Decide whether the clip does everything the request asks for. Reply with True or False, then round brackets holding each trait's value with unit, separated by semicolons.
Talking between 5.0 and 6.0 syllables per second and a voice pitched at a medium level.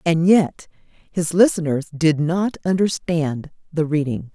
False (4.0 syllables/s; 165 Hz)